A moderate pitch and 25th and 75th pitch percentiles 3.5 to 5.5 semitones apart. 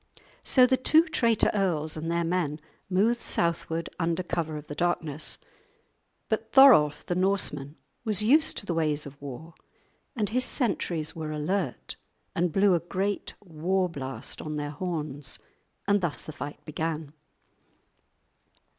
Yes: medium, 170 Hz; average, 4.7 semitones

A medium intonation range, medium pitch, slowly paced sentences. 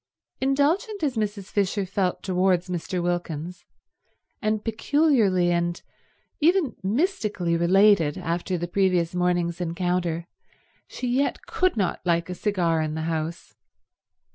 Yes: average, 4.0 semitones; medium, 180 Hz; slow, 120 wpm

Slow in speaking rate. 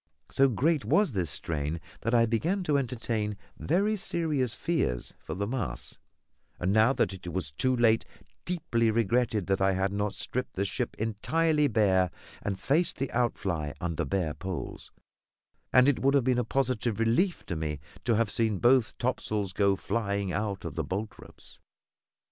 No: average, 165 wpm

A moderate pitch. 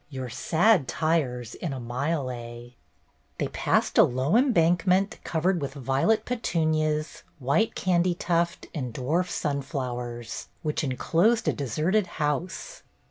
Yes: medium, 155 Hz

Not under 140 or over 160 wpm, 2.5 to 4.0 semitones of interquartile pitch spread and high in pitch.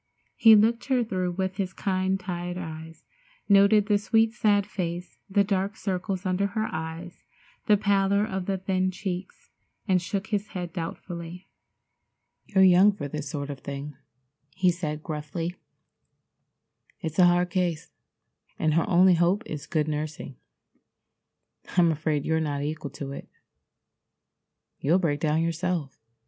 No: average, 145 wpm; average, 3.5 semitones; medium, 180 Hz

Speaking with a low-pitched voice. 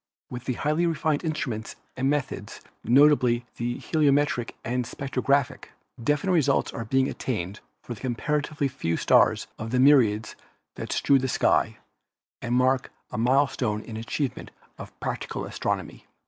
Yes: low, 130 Hz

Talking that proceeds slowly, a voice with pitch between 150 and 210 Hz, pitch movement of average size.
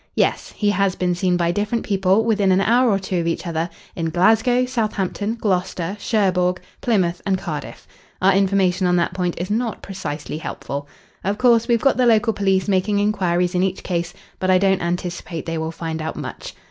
No: average, 195 wpm; high, 190 Hz; average, 3.0 semitones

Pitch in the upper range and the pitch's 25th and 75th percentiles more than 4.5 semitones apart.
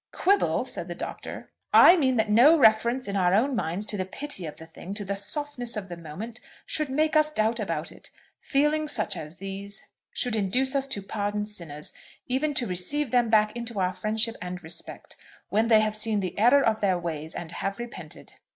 Yes: high, 215 Hz; average, 5.2 semitones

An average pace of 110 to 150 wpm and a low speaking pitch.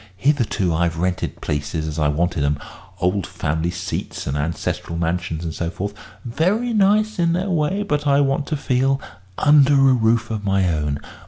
No: average, 175 wpm; low, 100 Hz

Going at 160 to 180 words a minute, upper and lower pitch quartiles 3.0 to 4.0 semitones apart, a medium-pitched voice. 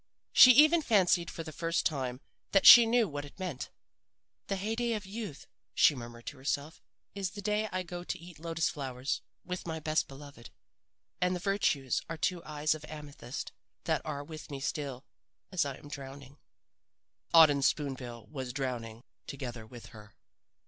No: average, 170 wpm; average, 5.1 semitones; medium, 150 Hz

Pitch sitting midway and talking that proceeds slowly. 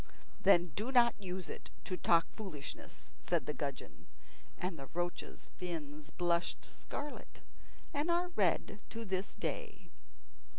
Yes: medium, 180 Hz; slow, 130 wpm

